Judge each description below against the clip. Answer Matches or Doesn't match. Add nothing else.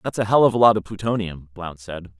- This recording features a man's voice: Matches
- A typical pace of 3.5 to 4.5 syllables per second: Doesn't match